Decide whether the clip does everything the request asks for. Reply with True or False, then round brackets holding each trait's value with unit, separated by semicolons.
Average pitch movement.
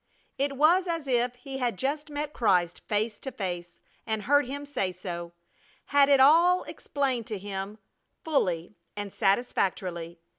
False (6.9 semitones)